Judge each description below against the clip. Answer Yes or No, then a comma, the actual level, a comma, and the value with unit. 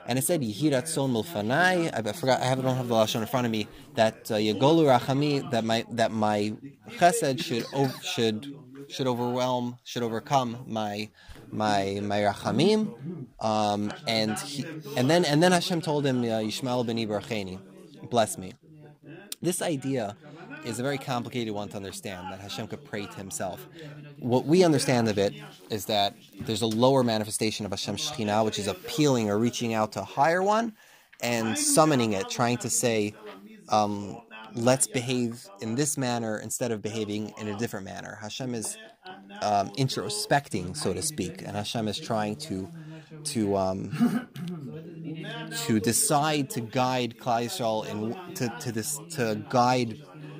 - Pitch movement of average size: Yes, average, 4.8 semitones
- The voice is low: Yes, low, 120 Hz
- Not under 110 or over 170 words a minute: Yes, average, 160 wpm